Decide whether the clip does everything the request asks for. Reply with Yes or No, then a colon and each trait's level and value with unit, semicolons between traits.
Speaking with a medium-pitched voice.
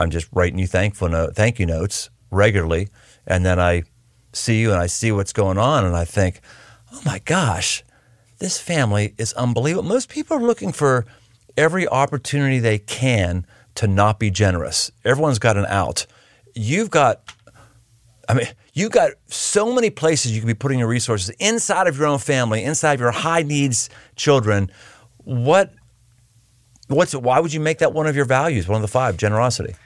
No: low, 120 Hz